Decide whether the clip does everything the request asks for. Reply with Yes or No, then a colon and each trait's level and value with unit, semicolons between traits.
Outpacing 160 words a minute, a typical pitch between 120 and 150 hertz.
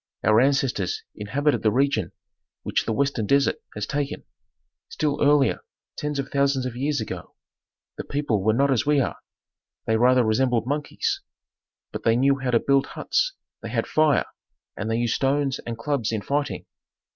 Yes: average, 170 wpm; low, 135 Hz